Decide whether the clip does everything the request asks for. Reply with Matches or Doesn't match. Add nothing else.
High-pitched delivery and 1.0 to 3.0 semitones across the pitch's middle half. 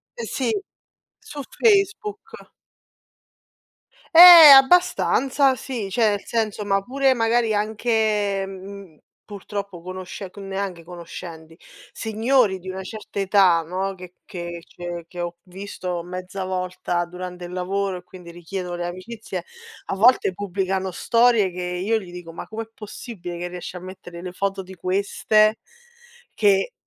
Doesn't match